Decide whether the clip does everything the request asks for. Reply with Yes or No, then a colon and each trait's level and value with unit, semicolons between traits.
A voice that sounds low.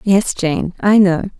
No: high, 190 Hz